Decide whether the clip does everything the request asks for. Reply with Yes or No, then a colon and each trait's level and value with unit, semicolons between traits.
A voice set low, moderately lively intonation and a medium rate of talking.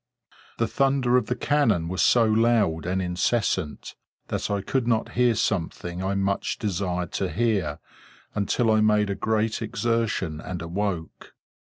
Yes: low, 105 Hz; average, 4.2 semitones; average, 150 wpm